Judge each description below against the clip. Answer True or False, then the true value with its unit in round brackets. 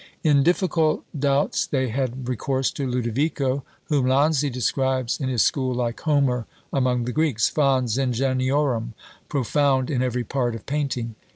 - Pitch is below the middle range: True (130 Hz)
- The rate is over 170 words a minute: False (145 wpm)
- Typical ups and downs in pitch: False (2.3 semitones)